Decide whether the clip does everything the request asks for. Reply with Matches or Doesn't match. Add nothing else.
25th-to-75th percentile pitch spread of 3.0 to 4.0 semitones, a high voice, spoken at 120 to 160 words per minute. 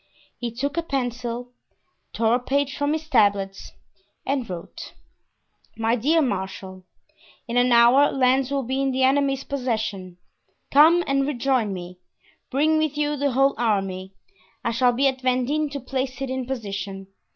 Matches